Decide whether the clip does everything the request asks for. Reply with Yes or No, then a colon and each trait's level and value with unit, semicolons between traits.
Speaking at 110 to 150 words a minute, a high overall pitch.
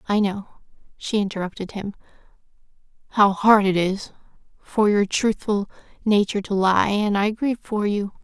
Yes: average, 145 wpm; high, 205 Hz